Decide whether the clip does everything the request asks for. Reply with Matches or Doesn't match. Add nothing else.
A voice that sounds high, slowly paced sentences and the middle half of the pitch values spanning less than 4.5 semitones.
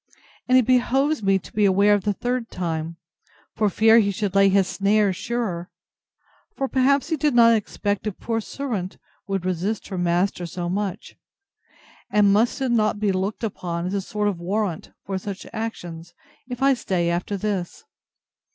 Doesn't match